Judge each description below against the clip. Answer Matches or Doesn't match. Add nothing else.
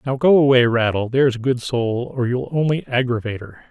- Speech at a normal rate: Doesn't match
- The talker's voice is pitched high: Doesn't match